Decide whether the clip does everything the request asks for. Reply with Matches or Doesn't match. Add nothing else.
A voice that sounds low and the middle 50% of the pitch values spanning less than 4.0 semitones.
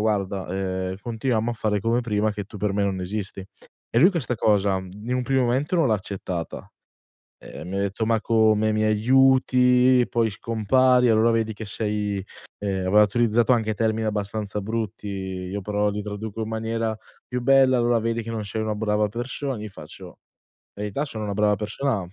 Matches